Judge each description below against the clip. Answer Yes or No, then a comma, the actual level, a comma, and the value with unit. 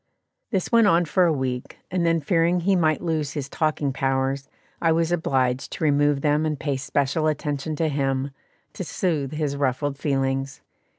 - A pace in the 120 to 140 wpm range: No, average, 175 wpm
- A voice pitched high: No, medium, 150 Hz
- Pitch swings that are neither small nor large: Yes, average, 3.3 semitones